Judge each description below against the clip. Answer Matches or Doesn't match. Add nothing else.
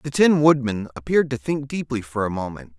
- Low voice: Matches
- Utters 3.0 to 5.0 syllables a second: Doesn't match